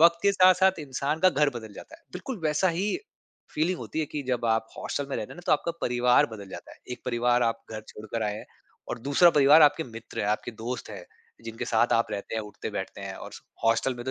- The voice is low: Yes, low, 125 Hz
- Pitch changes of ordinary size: No, wide, 5.7 semitones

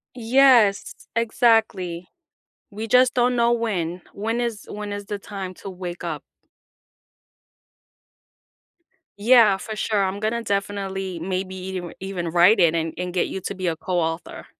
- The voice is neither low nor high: No, high, 195 Hz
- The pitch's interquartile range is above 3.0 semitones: Yes, average, 3.6 semitones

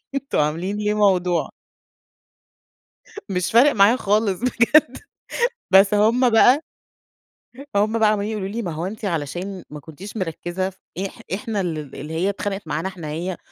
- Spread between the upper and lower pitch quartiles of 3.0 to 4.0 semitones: Yes, average, 3.7 semitones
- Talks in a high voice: Yes, high, 195 Hz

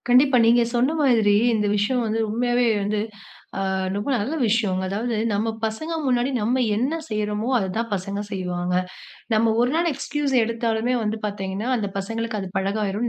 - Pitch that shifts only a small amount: No, average, 3.0 semitones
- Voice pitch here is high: Yes, high, 220 Hz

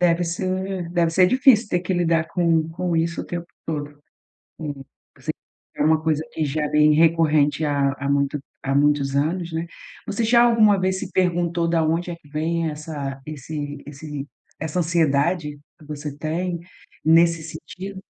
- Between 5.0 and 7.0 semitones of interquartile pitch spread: No, average, 2.8 semitones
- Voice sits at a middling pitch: Yes, medium, 160 Hz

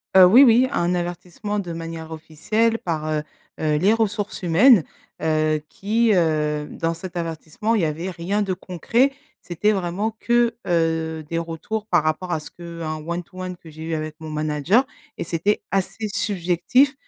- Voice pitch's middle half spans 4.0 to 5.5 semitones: Yes, average, 4.4 semitones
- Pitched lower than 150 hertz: No, medium, 175 Hz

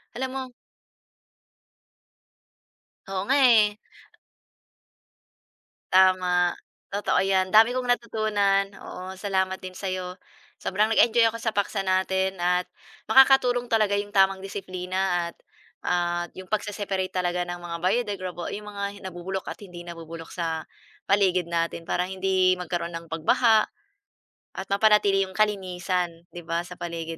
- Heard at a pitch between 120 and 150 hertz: No, high, 190 Hz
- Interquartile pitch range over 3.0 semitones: No, narrow, 2.5 semitones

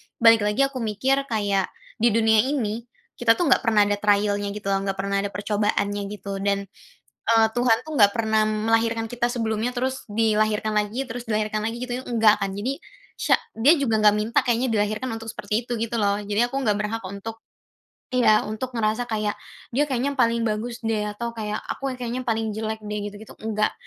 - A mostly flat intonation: Yes, narrow, 2.3 semitones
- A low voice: No, high, 220 Hz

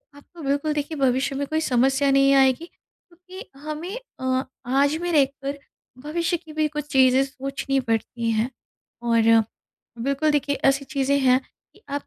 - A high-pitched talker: Yes, very high, 275 Hz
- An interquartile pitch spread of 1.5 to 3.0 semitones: Yes, narrow, 2.4 semitones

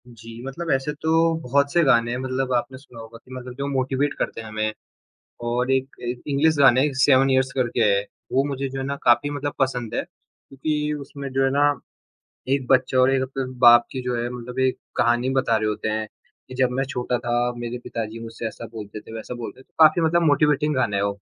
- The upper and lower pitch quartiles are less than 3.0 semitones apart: Yes, narrow, 2.6 semitones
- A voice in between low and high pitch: No, low, 130 Hz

